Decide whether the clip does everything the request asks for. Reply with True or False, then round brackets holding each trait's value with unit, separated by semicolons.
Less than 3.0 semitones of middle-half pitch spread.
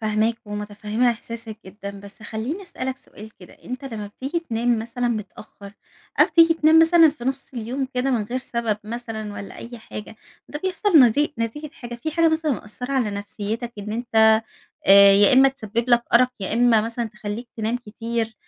False (3.5 semitones)